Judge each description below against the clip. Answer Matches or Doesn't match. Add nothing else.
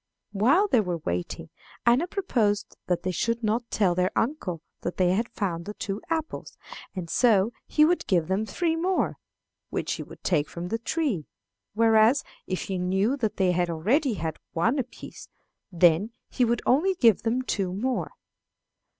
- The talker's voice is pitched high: Matches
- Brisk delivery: Doesn't match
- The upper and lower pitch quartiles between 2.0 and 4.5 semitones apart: Doesn't match